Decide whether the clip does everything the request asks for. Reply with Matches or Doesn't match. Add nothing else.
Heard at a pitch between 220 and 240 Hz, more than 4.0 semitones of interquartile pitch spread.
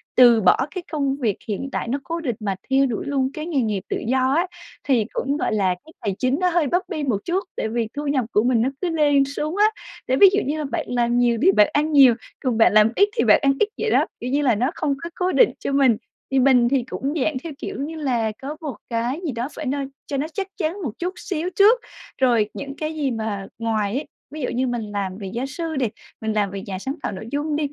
Doesn't match